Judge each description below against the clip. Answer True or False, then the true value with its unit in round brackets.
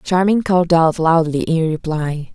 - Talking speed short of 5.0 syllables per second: True (4.4 syllables/s)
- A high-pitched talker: False (165 Hz)